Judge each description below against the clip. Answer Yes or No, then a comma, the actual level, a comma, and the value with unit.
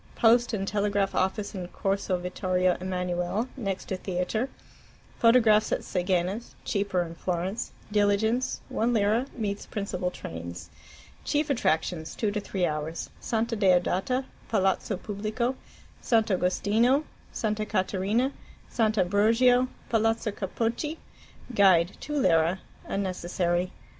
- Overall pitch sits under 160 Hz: No, high, 200 Hz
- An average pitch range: Yes, average, 3.7 semitones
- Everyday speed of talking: No, slow, 110 wpm